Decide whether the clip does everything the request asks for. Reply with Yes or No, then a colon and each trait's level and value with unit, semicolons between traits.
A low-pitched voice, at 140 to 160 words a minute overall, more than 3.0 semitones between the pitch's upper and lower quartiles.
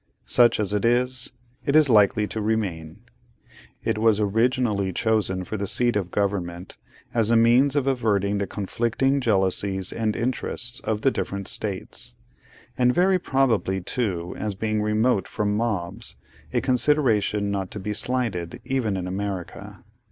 Yes: low, 105 Hz; average, 150 wpm; average, 3.6 semitones